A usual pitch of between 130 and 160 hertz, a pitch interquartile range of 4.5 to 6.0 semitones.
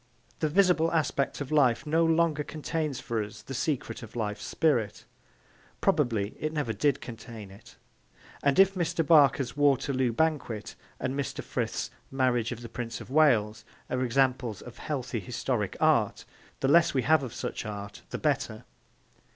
Yes: low, 135 Hz; average, 4.9 semitones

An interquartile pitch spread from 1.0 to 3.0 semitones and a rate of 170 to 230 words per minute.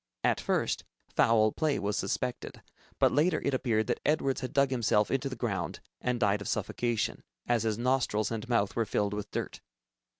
No: average, 3.7 semitones; average, 180 wpm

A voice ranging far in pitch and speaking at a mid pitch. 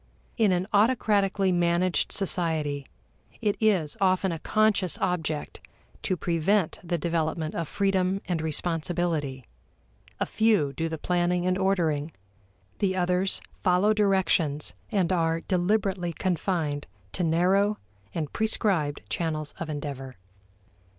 No: average, 3.3 semitones; medium, 175 Hz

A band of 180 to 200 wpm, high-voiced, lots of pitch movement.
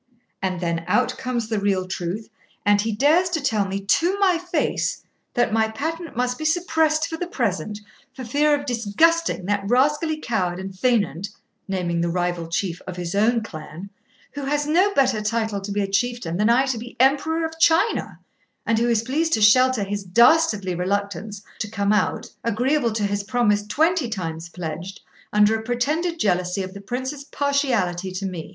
Yes: average, 185 wpm; high, 220 Hz; wide, 6.4 semitones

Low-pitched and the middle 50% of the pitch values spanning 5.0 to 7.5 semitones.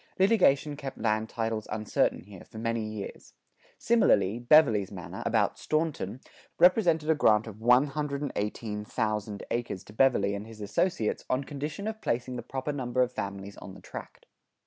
Yes: low, 120 Hz; wide, 5.4 semitones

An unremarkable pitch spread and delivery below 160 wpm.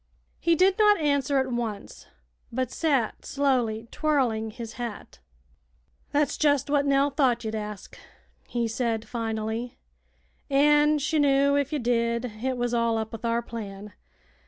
Yes: average, 3.8 semitones; average, 145 wpm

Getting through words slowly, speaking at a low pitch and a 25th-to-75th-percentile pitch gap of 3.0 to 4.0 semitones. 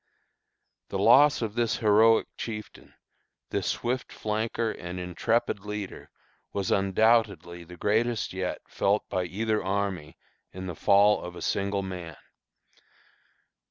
Yes: slow, 125 wpm; low, 100 Hz; average, 3.3 semitones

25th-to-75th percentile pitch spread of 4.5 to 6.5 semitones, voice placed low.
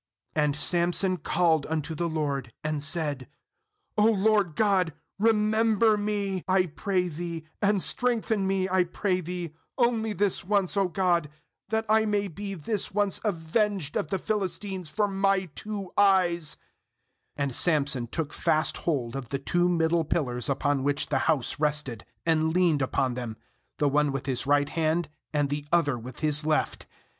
No: average, 5.1 semitones; medium, 170 Hz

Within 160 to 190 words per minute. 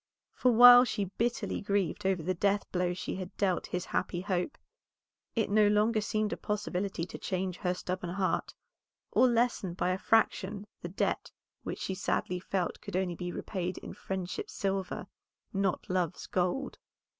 Yes: average, 165 wpm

